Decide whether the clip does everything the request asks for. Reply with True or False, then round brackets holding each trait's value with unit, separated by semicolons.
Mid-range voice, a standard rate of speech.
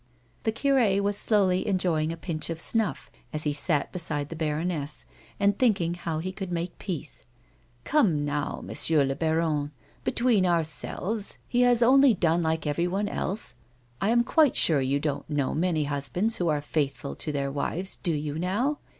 True (170 Hz; 175 wpm)